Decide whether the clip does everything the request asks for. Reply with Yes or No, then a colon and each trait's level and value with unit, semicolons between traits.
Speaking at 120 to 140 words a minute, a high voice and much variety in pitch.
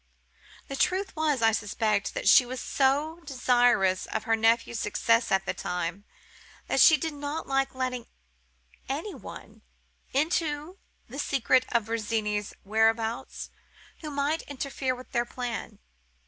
No: slow, 135 wpm; very high, 250 Hz; average, 4.3 semitones